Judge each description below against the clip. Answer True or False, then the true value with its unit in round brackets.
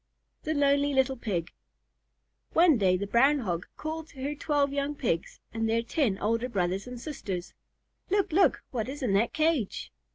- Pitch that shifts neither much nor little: False (5.9 semitones)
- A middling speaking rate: True (170 wpm)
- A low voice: False (260 Hz)